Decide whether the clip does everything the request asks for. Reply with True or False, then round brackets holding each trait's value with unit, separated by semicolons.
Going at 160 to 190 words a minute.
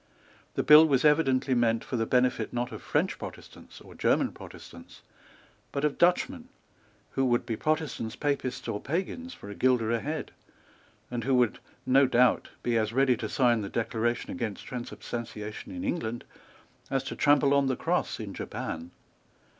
True (165 wpm)